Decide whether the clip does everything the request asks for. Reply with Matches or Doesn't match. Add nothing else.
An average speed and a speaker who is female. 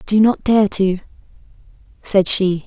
Matches